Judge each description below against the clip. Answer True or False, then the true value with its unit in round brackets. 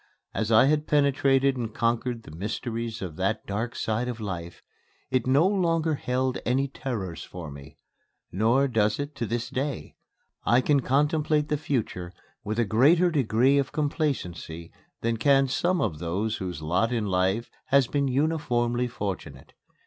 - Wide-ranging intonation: False (5.0 semitones)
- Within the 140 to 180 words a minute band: True (155 wpm)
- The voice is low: True (120 Hz)